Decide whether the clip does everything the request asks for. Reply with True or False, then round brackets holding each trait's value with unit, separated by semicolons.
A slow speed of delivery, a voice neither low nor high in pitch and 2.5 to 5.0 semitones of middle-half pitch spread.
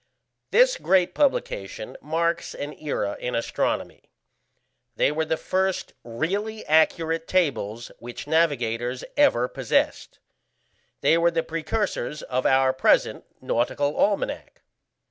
False (110 wpm; 160 Hz; 5.6 semitones)